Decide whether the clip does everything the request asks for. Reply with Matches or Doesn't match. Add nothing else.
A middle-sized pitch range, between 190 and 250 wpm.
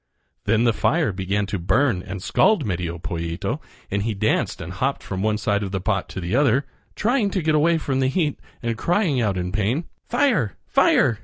Doesn't match